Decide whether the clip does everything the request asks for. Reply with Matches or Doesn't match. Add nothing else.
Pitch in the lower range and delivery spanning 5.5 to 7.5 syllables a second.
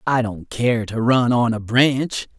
Doesn't match